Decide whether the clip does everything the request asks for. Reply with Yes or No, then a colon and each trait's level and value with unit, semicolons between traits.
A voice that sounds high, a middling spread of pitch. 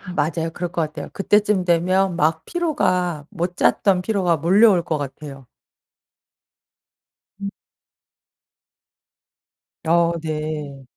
No: medium, 170 Hz; average, 3.6 semitones